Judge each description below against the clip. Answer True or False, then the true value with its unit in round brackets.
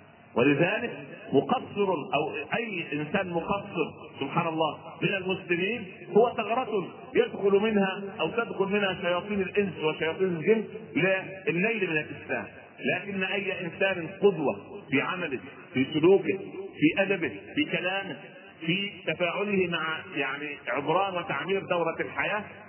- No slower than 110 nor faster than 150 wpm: True (115 wpm)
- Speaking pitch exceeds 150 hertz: True (190 Hz)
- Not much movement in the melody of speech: False (3.5 semitones)